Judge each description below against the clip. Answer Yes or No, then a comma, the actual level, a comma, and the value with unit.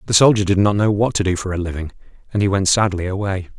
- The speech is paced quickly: Yes, fast, 270 wpm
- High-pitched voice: No, low, 100 Hz